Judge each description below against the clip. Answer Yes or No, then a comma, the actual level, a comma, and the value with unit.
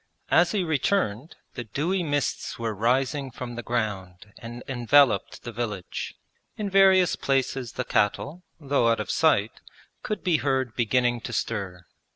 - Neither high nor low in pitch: No, low, 125 Hz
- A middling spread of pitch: Yes, average, 4.5 semitones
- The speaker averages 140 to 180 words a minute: Yes, average, 150 wpm